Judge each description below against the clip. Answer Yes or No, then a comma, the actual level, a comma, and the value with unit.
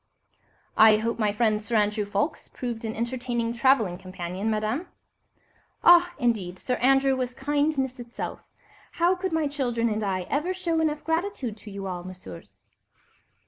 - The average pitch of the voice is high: Yes, high, 235 Hz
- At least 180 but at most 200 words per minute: No, average, 150 wpm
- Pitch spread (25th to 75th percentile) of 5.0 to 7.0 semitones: Yes, wide, 5.4 semitones